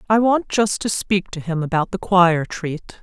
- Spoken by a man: No, female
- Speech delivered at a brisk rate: Yes, fast, 220 wpm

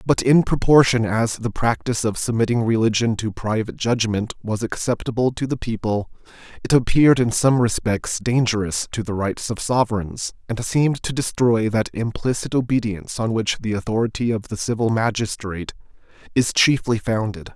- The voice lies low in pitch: Yes, low, 115 Hz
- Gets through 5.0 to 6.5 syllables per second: Yes, 5.3 syllables/s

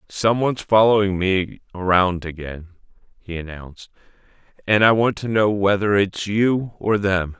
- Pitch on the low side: Yes, low, 100 Hz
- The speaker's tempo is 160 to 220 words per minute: No, average, 140 wpm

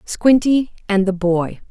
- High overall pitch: Yes, high, 205 Hz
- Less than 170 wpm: Yes, average, 140 wpm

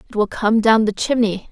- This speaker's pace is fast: Yes, fast, 240 wpm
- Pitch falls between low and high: No, high, 215 Hz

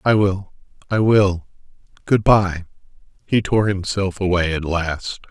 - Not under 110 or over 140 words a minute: Yes, slow, 135 wpm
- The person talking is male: Yes, male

